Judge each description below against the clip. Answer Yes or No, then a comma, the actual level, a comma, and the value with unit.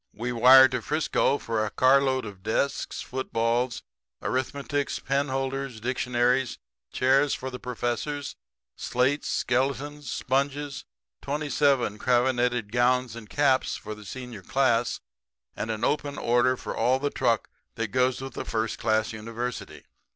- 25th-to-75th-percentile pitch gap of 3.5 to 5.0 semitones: No, narrow, 2.6 semitones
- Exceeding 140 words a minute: No, slow, 135 wpm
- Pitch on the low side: Yes, low, 125 Hz